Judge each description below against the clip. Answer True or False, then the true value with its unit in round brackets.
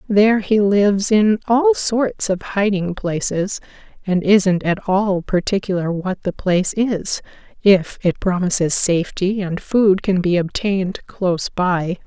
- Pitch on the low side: False (195 Hz)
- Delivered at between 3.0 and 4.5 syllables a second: True (4.1 syllables/s)